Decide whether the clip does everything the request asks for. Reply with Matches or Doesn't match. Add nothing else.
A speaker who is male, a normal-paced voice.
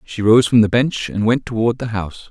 Doesn't match